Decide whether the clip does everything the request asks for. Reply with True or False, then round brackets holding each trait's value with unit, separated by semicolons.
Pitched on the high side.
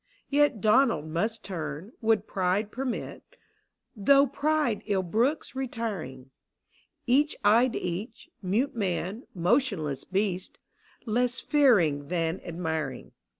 True (210 Hz)